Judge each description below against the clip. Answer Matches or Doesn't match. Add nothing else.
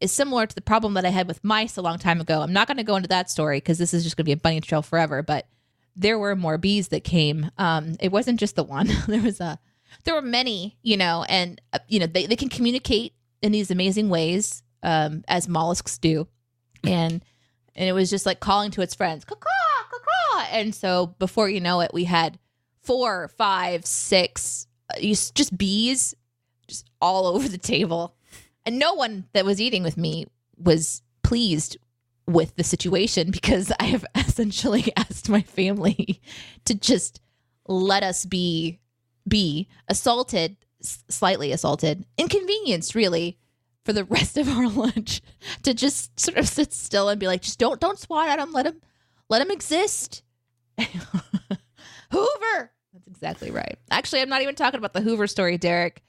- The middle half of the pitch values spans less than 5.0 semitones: Doesn't match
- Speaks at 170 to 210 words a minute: Matches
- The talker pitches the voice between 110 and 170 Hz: Doesn't match